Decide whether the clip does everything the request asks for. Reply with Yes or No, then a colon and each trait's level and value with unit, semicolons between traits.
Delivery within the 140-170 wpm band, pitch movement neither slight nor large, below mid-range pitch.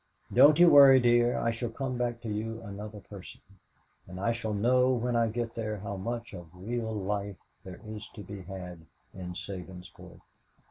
No: average, 180 wpm; average, 3.3 semitones; low, 110 Hz